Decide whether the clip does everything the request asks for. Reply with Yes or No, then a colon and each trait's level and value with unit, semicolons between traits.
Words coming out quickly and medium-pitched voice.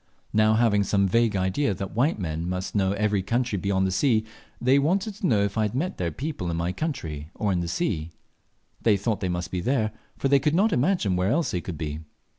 No: fast, 235 wpm; low, 100 Hz